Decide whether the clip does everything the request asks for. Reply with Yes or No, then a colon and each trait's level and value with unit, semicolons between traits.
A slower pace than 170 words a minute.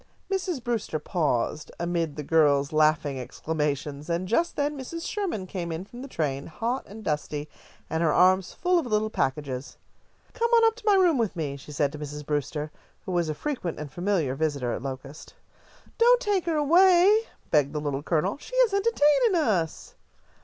No: average, 180 wpm